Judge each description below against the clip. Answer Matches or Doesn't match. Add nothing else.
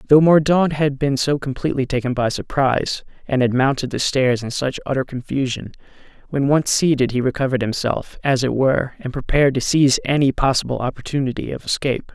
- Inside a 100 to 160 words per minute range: Doesn't match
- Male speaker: Matches